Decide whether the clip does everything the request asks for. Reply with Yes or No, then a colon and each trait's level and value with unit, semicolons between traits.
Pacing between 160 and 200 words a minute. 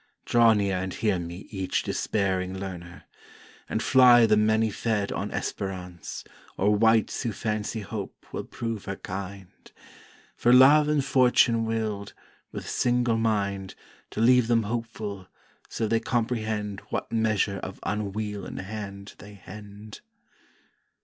No: slow, 135 wpm